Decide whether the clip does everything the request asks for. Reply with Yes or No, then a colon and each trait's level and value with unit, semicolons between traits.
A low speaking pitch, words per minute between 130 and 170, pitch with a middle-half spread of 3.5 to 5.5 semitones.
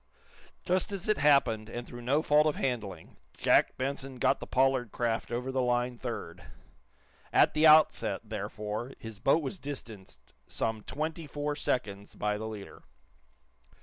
Yes: low, 125 Hz; average, 150 wpm; average, 4.7 semitones